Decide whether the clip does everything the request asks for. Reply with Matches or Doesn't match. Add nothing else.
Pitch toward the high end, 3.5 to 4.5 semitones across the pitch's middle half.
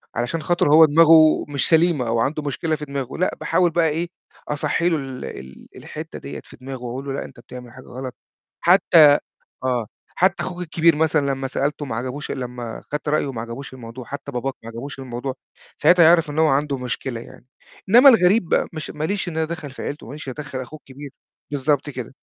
Doesn't match